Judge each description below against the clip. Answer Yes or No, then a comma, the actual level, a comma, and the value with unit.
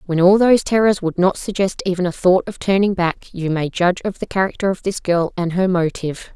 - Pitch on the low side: No, medium, 185 Hz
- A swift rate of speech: Yes, fast, 235 wpm